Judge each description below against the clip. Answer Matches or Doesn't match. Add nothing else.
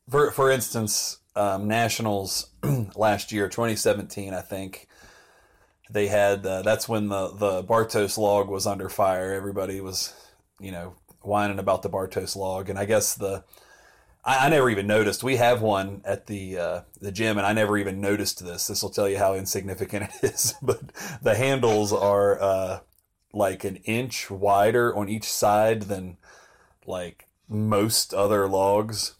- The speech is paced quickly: Doesn't match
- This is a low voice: Matches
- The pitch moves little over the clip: Matches